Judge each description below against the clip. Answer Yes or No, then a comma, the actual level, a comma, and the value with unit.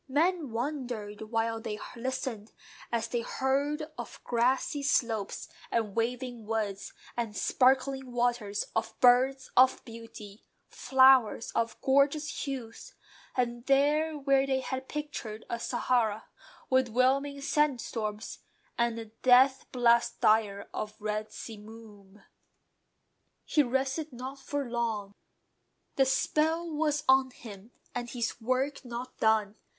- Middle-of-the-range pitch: No, high, 245 Hz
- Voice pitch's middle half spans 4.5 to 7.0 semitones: No, average, 3.2 semitones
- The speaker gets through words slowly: Yes, slow, 120 wpm